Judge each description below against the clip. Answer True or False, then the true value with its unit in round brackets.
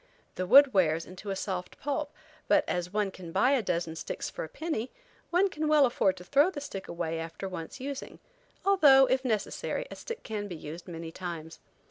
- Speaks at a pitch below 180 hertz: False (195 Hz)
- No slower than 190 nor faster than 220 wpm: True (200 wpm)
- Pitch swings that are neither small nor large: False (8.4 semitones)